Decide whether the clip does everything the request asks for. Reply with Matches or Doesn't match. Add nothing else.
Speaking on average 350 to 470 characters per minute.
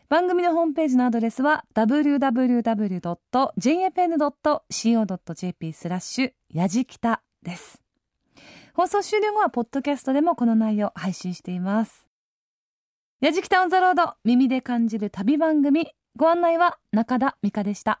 Doesn't match